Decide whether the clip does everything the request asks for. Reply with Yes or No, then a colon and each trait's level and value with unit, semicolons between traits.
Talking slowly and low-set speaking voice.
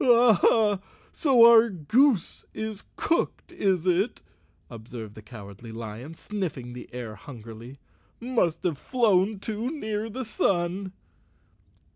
No: slow, 120 wpm; high, 190 Hz